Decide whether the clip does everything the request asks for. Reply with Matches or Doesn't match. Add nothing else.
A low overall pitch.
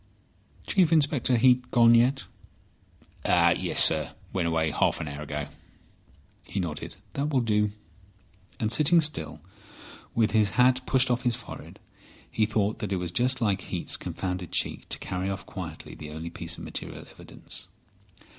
Matches